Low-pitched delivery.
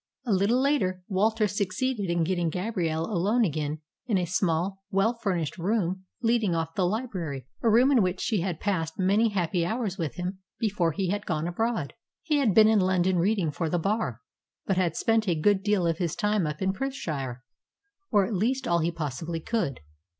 No: high, 190 Hz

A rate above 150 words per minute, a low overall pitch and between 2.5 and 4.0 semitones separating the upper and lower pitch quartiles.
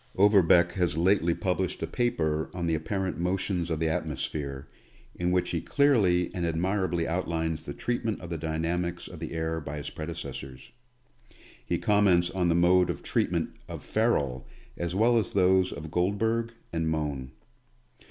Yes: average, 160 wpm; very low, 85 Hz; average, 2.8 semitones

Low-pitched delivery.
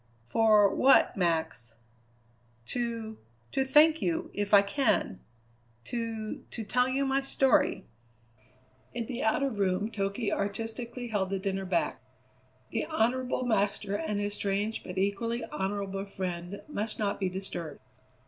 No: high, 210 Hz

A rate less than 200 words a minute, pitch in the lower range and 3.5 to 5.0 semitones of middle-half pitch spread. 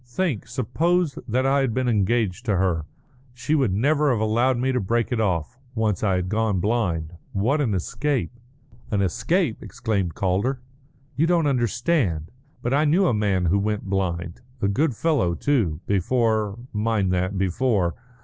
No: average, 165 wpm; low, 110 Hz; wide, 5.4 semitones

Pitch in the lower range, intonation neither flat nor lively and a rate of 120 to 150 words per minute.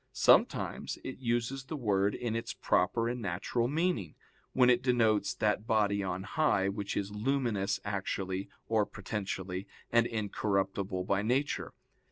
Yes: low, 105 Hz; average, 3.7 semitones; average, 140 wpm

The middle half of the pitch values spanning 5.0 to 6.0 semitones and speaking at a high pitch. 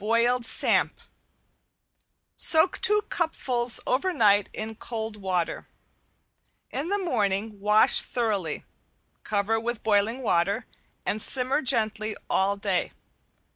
No: average, 3.5 semitones; high, 220 Hz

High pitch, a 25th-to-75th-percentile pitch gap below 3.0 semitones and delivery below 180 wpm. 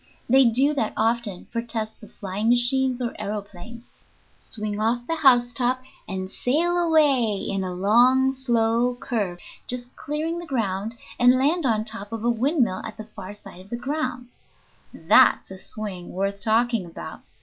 No: high, 235 Hz; average, 3.7 semitones; average, 160 wpm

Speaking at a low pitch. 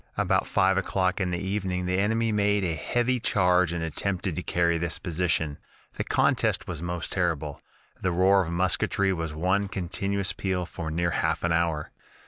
Yes: very low, 90 Hz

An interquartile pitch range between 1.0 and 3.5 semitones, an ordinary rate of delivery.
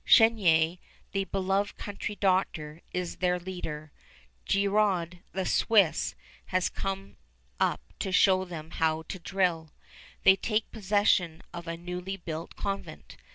No: average, 2.7 semitones; slow, 125 wpm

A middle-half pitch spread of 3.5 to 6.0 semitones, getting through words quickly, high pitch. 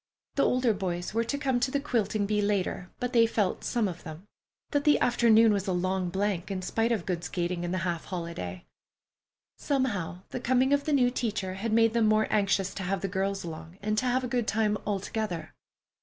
Yes: average, 4.3 semitones; fast, 210 wpm; high, 205 Hz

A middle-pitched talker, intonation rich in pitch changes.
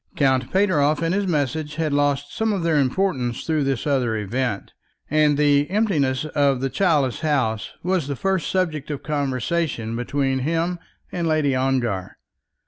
No: medium, 145 Hz; average, 3.8 semitones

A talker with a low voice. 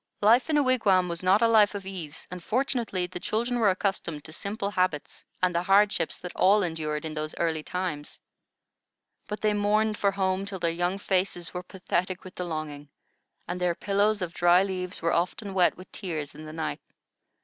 No: medium, 185 Hz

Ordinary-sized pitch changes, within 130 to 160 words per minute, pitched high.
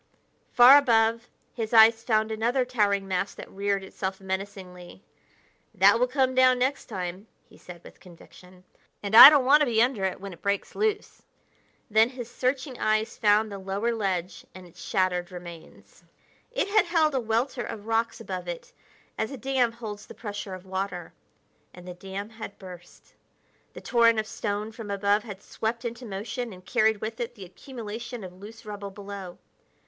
No: average, 3.8 semitones; average, 175 wpm; high, 215 Hz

